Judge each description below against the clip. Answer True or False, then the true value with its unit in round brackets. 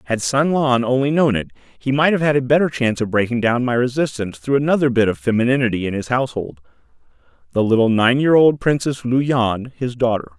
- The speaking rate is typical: False (210 wpm)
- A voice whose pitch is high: False (125 Hz)